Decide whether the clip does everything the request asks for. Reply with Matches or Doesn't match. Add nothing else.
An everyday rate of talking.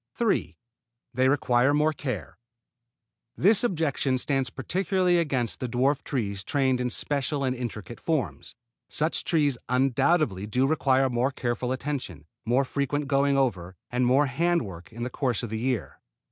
Matches